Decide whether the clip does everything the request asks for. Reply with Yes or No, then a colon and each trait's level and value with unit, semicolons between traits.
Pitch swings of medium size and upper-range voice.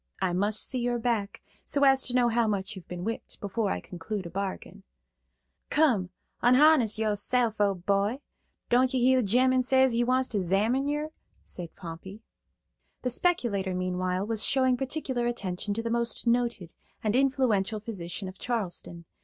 Yes: average, 4.6 semitones; high, 225 Hz